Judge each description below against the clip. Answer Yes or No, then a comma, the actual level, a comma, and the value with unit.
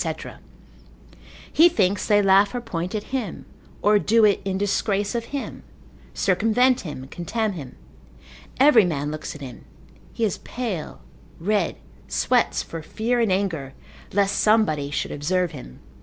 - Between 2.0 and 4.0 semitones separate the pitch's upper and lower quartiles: No, average, 5.1 semitones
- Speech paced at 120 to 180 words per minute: Yes, average, 140 wpm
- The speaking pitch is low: No, high, 200 Hz